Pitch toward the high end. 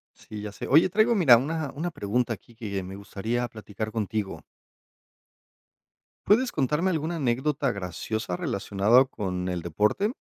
No: low, 115 Hz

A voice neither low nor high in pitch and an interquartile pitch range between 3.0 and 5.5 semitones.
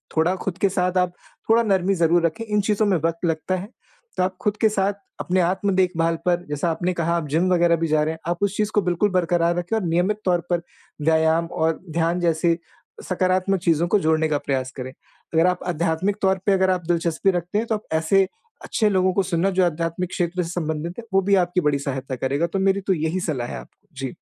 No: medium, 175 Hz; narrow, 2.6 semitones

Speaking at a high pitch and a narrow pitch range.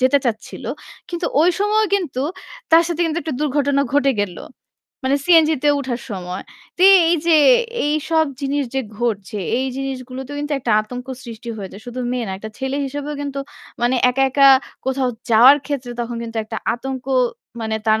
No: very high, 265 Hz; average, 3.5 semitones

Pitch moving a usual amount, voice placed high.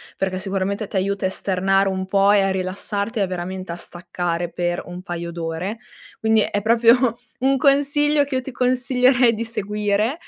Yes: average, 4.4 semitones; high, 200 Hz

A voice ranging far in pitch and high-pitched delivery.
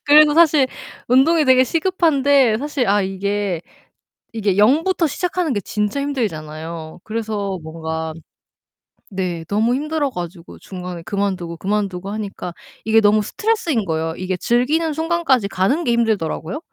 Yes: wide, 7.5 semitones; high, 215 Hz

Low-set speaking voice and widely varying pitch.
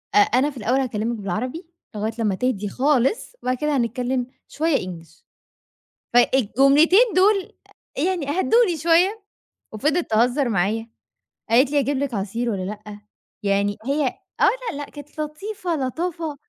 No: very high, 260 Hz; wide, 5.9 semitones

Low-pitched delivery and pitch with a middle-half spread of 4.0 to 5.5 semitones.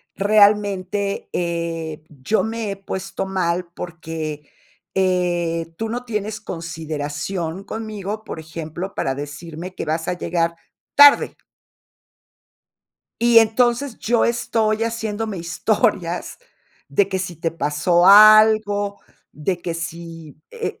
No: medium, 185 Hz; average, 4.4 semitones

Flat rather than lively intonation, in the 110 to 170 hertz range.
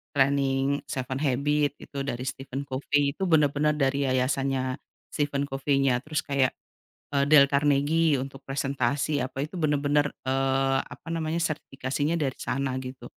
Yes: narrow, 1.5 semitones; medium, 140 Hz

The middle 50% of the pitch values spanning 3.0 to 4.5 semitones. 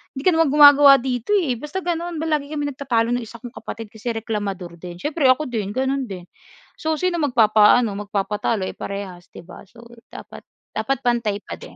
No: wide, 5.6 semitones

